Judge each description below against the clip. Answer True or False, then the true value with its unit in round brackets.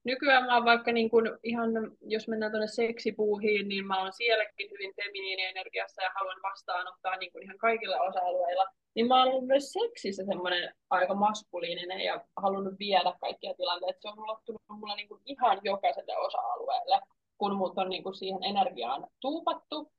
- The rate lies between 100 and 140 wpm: False (155 wpm)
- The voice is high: True (210 Hz)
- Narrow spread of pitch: False (3.7 semitones)